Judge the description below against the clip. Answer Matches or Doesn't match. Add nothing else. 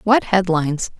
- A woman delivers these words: Matches